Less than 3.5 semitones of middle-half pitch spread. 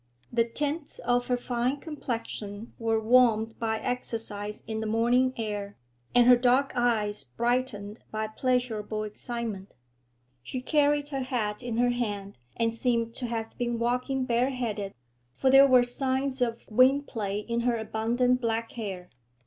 Yes: narrow, 2.4 semitones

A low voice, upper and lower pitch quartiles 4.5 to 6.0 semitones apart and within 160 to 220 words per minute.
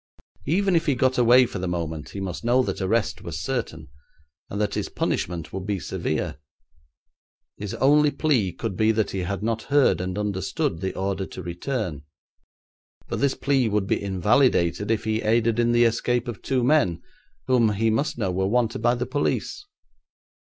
Yes: low, 110 Hz; average, 4.8 semitones; average, 180 wpm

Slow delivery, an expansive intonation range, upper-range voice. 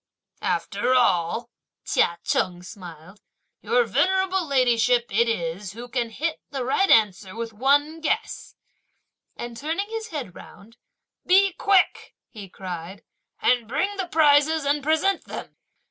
Yes: slow, 130 wpm; wide, 7.5 semitones; very high, 250 Hz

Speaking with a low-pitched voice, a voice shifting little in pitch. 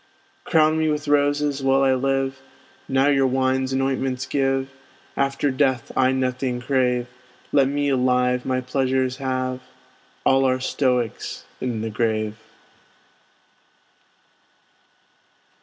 Yes: low, 130 Hz; narrow, 1.2 semitones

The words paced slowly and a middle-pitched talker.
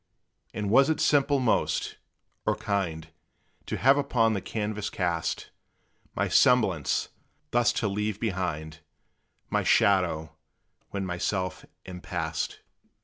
No: slow, 115 wpm; low, 100 Hz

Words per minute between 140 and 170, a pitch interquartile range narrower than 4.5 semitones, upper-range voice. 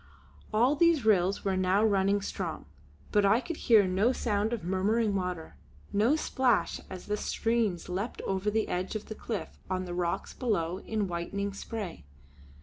Yes: average, 165 wpm; average, 3.1 semitones; high, 200 Hz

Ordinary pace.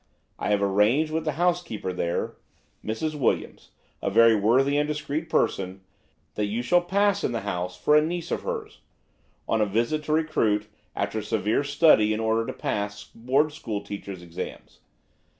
Yes: average, 160 wpm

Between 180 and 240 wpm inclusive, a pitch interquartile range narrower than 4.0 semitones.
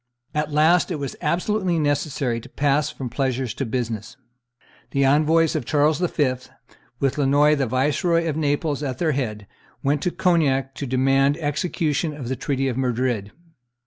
No: average, 160 wpm; average, 2.7 semitones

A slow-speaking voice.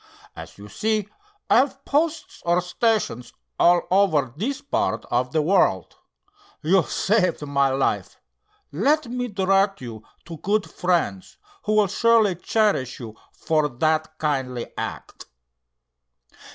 Yes: slow, 125 wpm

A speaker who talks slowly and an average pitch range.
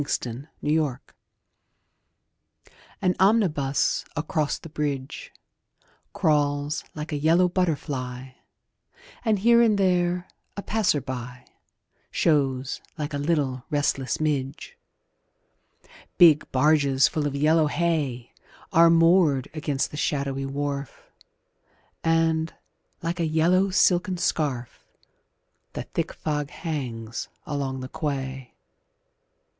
Yes: slow, 105 wpm; average, 3.4 semitones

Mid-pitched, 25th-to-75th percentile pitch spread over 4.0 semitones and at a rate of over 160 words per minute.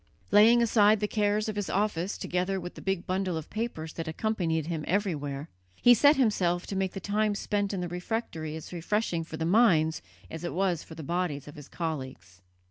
Yes: medium, 180 Hz; average, 4.4 semitones; fast, 205 wpm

